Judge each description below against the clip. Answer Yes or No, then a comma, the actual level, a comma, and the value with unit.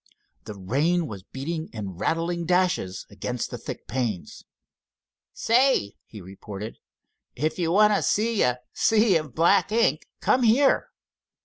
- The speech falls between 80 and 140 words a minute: Yes, slow, 135 wpm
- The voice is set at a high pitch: No, medium, 160 Hz